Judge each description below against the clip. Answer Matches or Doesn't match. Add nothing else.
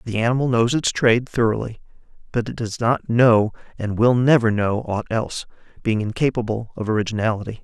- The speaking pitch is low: Matches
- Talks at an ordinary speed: Matches